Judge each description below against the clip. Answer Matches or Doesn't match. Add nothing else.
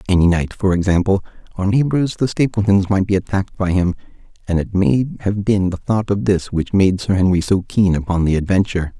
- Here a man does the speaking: Matches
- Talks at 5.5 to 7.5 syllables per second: Matches